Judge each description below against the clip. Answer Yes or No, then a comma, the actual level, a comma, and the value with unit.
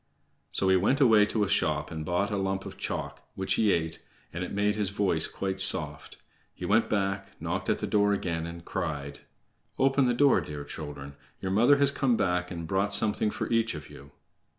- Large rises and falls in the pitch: No, average, 4.1 semitones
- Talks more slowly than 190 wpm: No, fast, 205 wpm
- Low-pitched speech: Yes, very low, 95 Hz